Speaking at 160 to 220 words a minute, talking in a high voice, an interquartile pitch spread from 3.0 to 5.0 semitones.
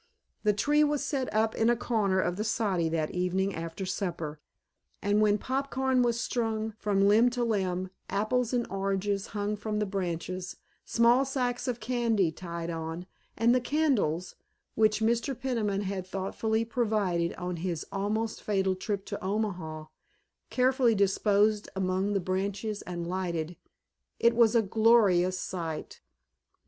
No: average, 150 wpm; high, 205 Hz; average, 3.9 semitones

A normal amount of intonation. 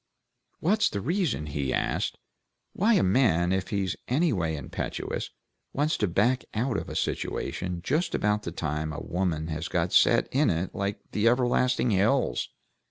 No: wide, 7.1 semitones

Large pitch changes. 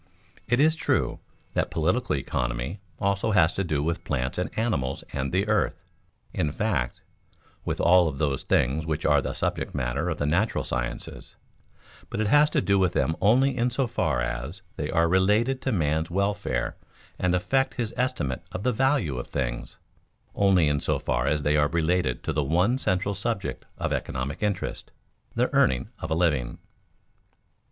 Yes: wide, 6.6 semitones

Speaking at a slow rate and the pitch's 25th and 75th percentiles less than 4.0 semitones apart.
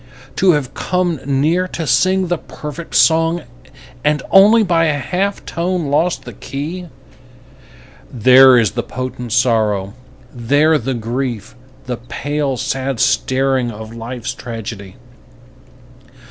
No: slow, 120 wpm; wide, 5.5 semitones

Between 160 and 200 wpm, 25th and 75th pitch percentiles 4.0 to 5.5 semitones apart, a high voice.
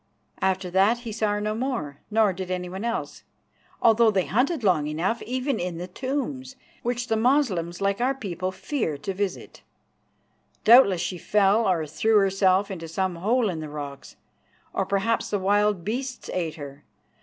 Yes: average, 165 wpm; average, 4.5 semitones; high, 200 Hz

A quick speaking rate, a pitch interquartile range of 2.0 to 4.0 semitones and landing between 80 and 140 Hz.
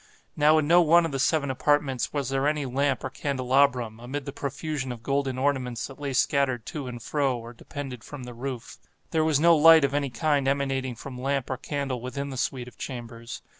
Yes: fast, 210 wpm; narrow, 2.4 semitones; low, 135 Hz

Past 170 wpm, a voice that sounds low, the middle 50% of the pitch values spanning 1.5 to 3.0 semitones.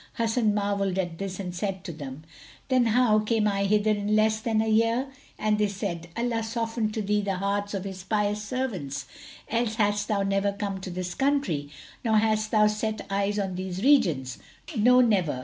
No: average, 190 wpm; high, 210 Hz; narrow, 2.5 semitones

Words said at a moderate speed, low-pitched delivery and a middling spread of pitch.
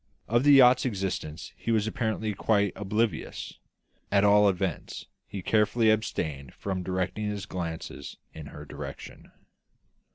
No: slow, 130 wpm; low, 100 Hz; average, 3.2 semitones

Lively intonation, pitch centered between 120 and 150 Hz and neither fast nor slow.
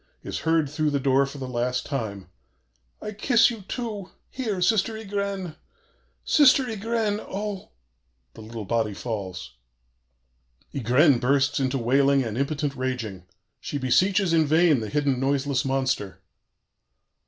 No: wide, 7.4 semitones; medium, 140 Hz; slow, 130 wpm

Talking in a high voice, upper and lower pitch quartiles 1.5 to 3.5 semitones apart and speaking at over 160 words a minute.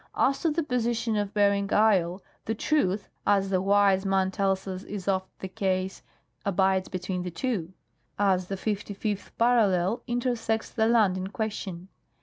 No: high, 200 Hz; average, 2.7 semitones; average, 150 wpm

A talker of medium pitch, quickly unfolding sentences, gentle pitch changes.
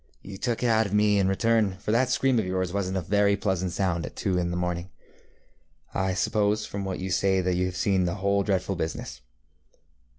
No: very low, 95 Hz; fast, 220 wpm; narrow, 2.0 semitones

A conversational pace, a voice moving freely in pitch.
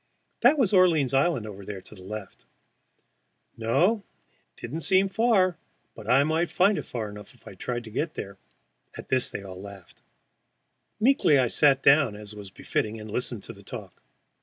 Yes: average, 185 wpm; wide, 8.7 semitones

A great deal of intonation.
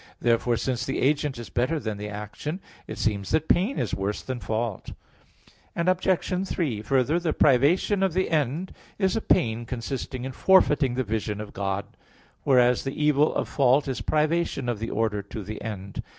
Yes: wide, 5.7 semitones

